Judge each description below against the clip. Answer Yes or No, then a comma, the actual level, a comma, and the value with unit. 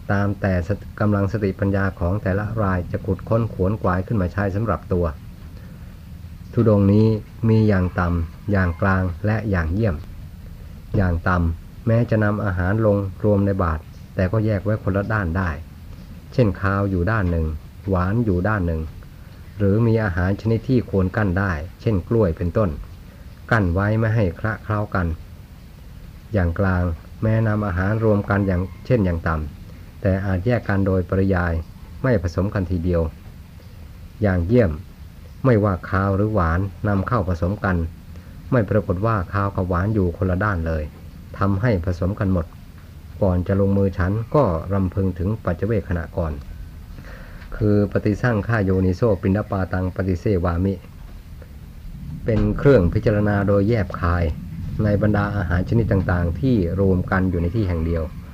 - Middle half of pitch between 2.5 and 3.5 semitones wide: Yes, average, 3.0 semitones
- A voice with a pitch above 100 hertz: No, very low, 95 Hz